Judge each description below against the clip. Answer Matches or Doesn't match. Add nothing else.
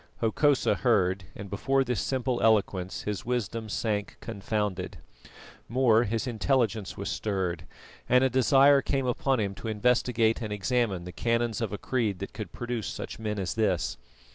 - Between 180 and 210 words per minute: Doesn't match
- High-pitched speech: Doesn't match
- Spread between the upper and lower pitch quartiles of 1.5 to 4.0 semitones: Matches